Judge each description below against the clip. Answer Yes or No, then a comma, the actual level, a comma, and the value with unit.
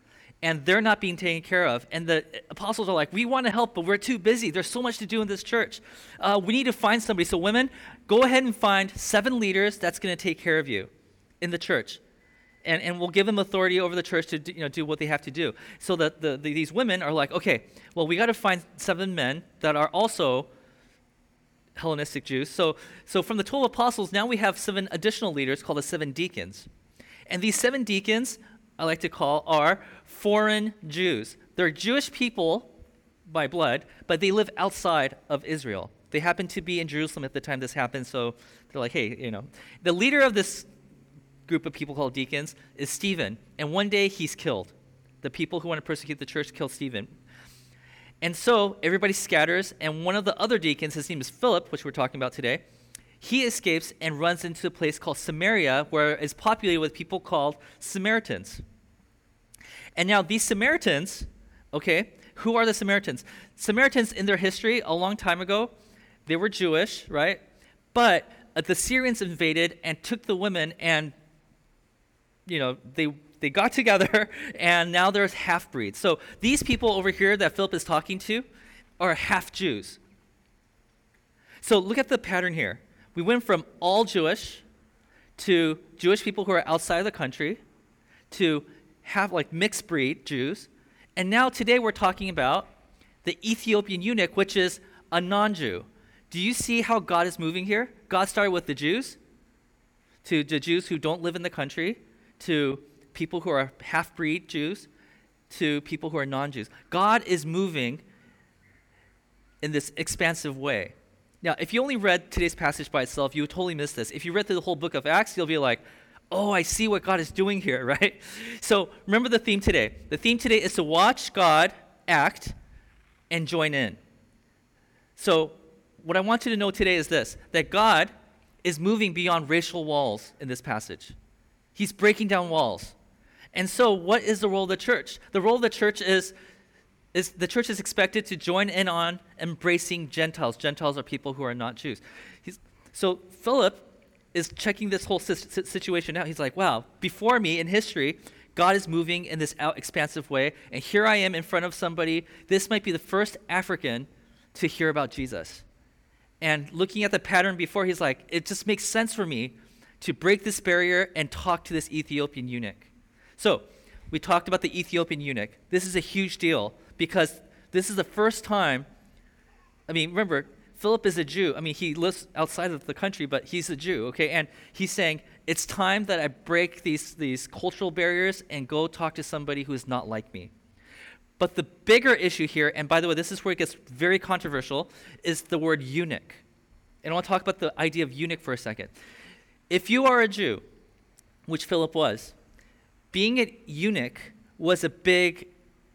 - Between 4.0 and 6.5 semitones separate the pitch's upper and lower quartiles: Yes, average, 4.7 semitones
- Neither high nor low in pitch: Yes, medium, 175 Hz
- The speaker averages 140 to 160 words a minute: No, average, 190 wpm